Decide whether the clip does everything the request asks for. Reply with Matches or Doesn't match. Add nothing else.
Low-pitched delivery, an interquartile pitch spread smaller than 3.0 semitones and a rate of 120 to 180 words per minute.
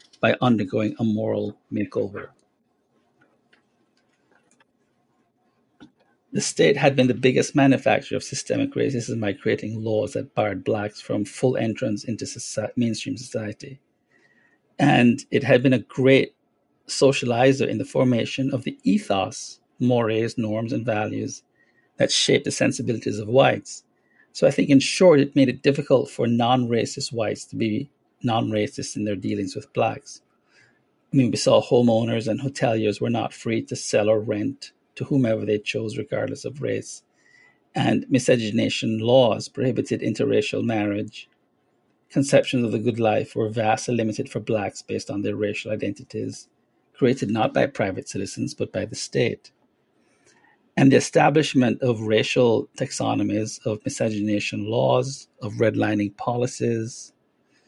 Doesn't match